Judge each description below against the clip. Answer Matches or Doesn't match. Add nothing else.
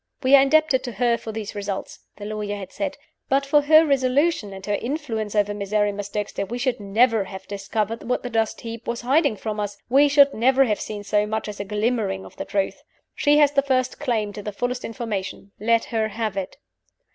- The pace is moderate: Doesn't match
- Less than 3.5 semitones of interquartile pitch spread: Doesn't match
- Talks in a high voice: Matches